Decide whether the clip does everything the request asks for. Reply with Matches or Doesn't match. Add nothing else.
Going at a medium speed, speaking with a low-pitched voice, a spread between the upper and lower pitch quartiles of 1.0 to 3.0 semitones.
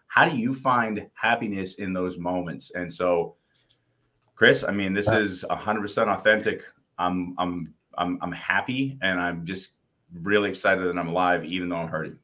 Matches